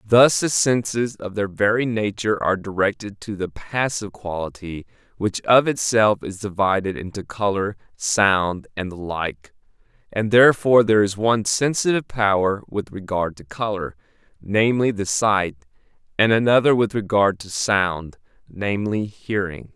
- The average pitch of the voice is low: Yes, low, 105 Hz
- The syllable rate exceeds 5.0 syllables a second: No, 4.8 syllables/s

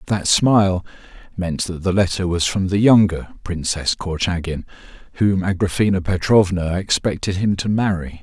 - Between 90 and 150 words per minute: Yes, average, 140 wpm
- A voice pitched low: Yes, very low, 95 Hz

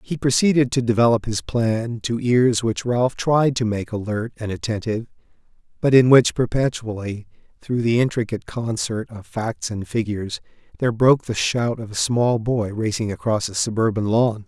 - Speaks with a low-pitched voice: Yes, low, 115 Hz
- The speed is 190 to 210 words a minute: No, average, 170 wpm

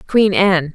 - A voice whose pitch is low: No, medium, 185 Hz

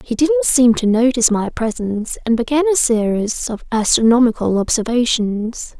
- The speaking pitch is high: Yes, high, 240 Hz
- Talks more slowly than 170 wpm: Yes, average, 145 wpm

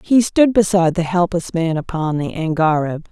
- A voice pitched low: No, medium, 175 Hz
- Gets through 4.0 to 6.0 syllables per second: Yes, 5.0 syllables/s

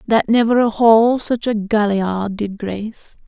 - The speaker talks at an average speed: Yes, average, 165 wpm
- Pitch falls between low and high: No, high, 220 Hz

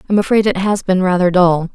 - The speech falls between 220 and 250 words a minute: Yes, fast, 240 wpm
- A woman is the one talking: Yes, female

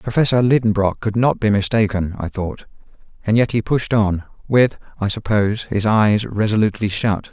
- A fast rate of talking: No, average, 165 wpm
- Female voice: No, male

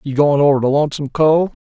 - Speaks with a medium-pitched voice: Yes, medium, 145 Hz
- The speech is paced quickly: Yes, fast, 220 wpm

